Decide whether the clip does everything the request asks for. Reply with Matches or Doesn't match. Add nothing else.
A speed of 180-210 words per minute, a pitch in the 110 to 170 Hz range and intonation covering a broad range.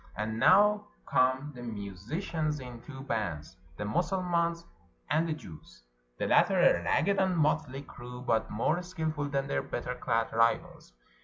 Doesn't match